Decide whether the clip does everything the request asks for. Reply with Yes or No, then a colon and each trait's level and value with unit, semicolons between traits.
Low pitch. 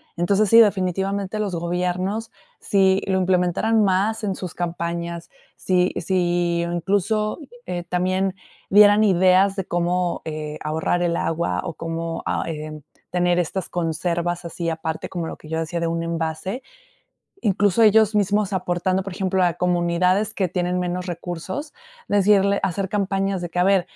No: medium, 180 Hz